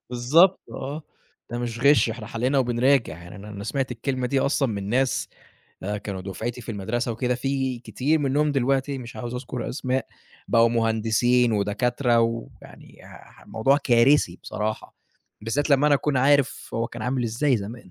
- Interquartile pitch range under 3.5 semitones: Yes, average, 3.1 semitones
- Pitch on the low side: Yes, low, 120 Hz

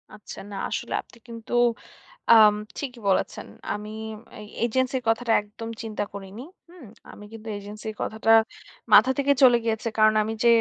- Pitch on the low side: No, high, 225 Hz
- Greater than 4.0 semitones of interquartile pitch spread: No, narrow, 2.5 semitones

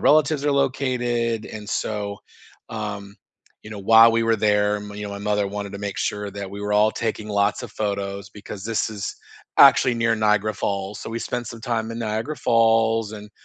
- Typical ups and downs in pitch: No, narrow, 2.0 semitones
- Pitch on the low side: Yes, low, 105 Hz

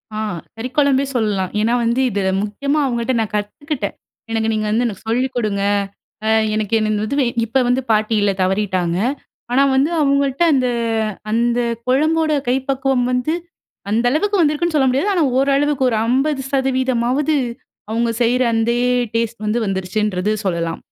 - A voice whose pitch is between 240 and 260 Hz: Yes, high, 245 Hz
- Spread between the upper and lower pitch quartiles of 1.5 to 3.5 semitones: No, average, 4.3 semitones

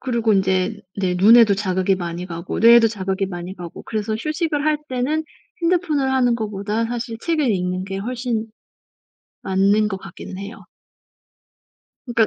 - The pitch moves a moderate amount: Yes, average, 4.2 semitones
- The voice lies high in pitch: Yes, high, 215 Hz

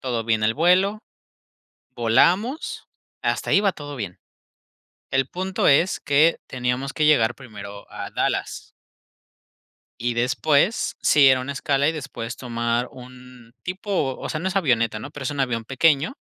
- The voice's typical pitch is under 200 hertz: Yes, low, 135 Hz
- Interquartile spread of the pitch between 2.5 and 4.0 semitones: No, average, 4.8 semitones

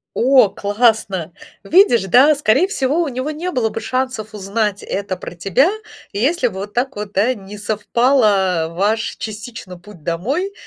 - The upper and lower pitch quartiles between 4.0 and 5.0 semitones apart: Yes, average, 4.7 semitones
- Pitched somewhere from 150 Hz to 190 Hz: No, high, 220 Hz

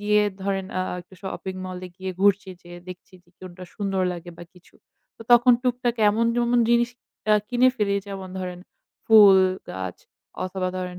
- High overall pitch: Yes, high, 195 Hz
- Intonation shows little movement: No, average, 3.2 semitones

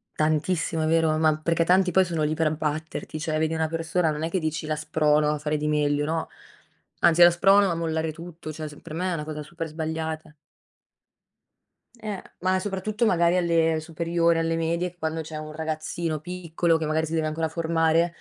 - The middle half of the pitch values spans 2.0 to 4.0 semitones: No, narrow, 1.4 semitones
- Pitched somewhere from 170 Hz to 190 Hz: No, medium, 160 Hz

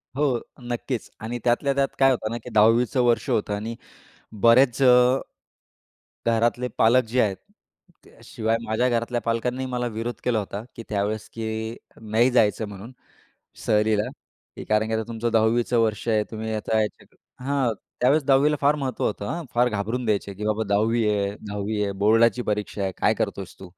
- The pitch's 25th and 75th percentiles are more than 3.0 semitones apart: No, narrow, 2.4 semitones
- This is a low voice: Yes, low, 115 Hz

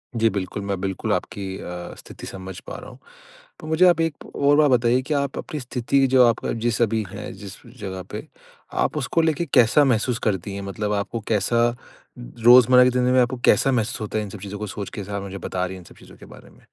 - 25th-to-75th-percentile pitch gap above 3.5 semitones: Yes, average, 4.4 semitones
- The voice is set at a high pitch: No, low, 115 Hz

